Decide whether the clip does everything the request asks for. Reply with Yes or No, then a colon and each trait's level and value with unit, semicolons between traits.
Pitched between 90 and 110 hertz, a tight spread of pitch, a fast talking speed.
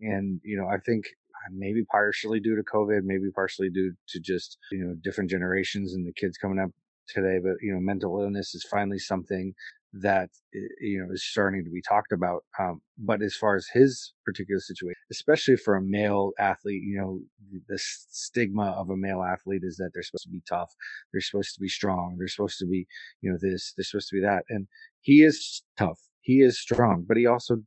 Yes: low, 100 Hz; narrow, 1.8 semitones; fast, 210 wpm